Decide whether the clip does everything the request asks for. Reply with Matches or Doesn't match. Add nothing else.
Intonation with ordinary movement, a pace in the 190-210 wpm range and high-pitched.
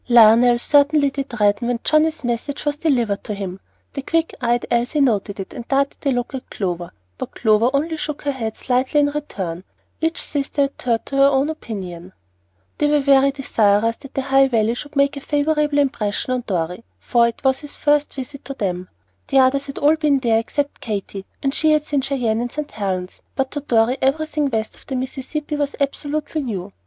Matches